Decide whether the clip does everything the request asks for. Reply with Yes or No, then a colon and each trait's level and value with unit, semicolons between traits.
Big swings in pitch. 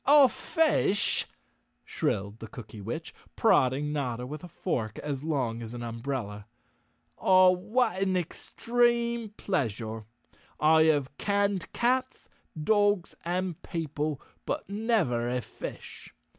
Yes: wide, 8.7 semitones